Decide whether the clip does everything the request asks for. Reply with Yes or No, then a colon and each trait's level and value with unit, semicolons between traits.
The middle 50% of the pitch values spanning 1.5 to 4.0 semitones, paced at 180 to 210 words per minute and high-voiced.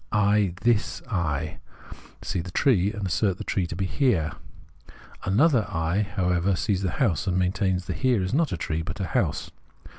No: average, 3.2 semitones; average, 185 wpm; very low, 95 Hz